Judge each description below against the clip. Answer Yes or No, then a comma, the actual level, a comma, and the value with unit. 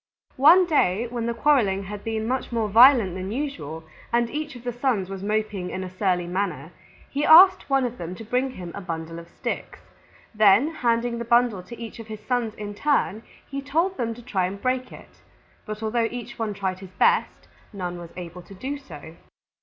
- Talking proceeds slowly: No, fast, 205 wpm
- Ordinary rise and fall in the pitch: Yes, average, 4.9 semitones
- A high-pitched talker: Yes, high, 225 Hz